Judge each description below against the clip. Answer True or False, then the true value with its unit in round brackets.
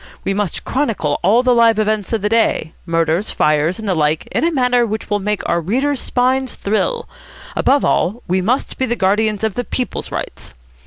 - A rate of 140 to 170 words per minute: False (200 wpm)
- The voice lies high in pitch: True (215 Hz)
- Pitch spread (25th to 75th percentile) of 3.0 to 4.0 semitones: False (4.8 semitones)